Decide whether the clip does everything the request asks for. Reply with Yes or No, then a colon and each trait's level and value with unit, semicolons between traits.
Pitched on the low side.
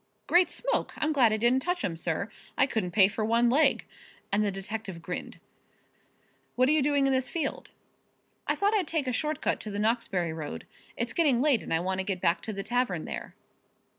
No: high, 230 Hz